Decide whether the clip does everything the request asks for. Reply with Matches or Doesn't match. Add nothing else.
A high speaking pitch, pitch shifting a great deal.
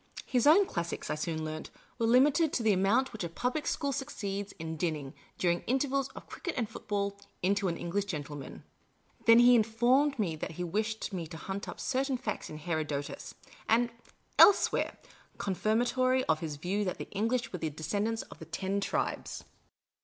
Matches